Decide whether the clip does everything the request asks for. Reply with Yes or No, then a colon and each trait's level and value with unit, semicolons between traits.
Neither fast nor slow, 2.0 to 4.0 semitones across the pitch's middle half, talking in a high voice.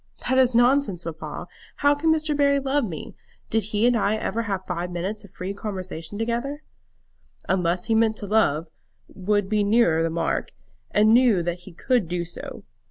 No: average, 180 wpm; average, 5.2 semitones; high, 210 Hz